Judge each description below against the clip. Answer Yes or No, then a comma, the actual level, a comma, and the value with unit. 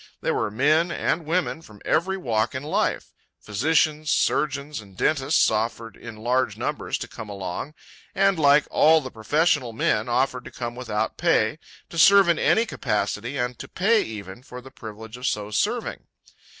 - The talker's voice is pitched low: Yes, low, 130 Hz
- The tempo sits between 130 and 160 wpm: No, average, 170 wpm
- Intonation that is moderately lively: No, wide, 5.9 semitones